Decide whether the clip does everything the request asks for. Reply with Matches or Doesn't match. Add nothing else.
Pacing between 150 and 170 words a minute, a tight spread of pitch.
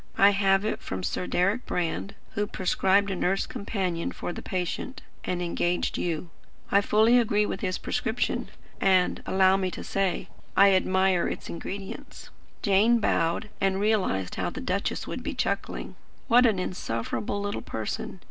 Matches